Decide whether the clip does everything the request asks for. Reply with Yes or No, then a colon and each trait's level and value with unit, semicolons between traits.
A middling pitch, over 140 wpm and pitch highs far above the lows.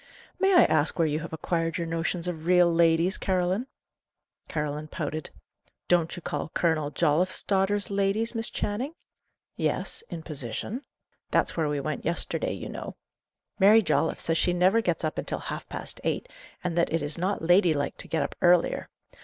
No: medium, 170 Hz; average, 175 wpm; average, 3.4 semitones